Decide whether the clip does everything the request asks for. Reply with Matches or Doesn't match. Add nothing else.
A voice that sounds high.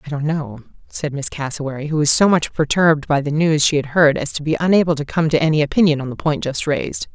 Doesn't match